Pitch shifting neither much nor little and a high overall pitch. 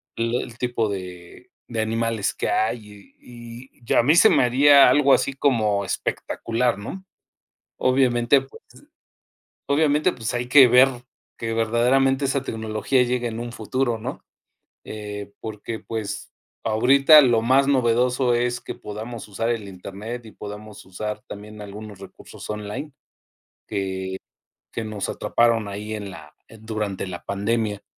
No: average, 3.0 semitones; low, 115 Hz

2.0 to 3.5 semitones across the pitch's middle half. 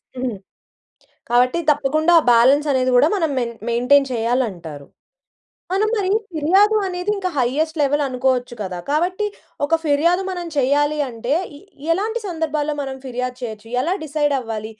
No: average, 4.8 semitones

